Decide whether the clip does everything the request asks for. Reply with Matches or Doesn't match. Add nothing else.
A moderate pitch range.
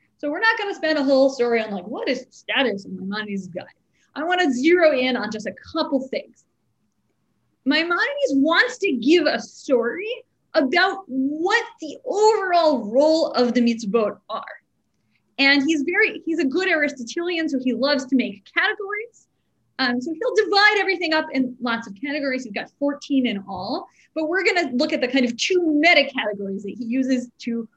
Doesn't match